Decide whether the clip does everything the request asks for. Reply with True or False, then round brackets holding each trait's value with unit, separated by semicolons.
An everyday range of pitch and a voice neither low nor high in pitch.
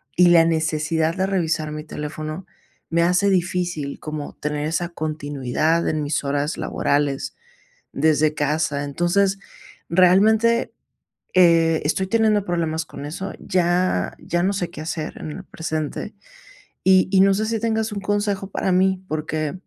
True (3.6 semitones; 170 Hz)